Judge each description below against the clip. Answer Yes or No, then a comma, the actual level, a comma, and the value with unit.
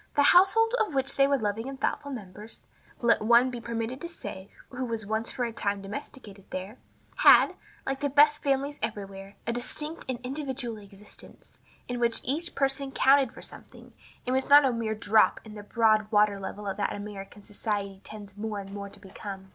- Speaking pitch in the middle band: No, high, 230 Hz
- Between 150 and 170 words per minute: No, average, 185 wpm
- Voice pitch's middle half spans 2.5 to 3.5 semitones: No, average, 4.7 semitones